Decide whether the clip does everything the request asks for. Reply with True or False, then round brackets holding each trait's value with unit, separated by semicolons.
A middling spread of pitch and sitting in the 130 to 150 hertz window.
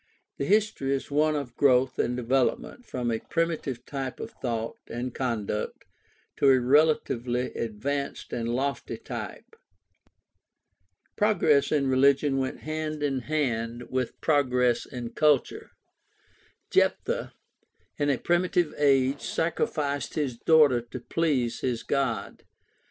True (3.3 semitones; 135 Hz)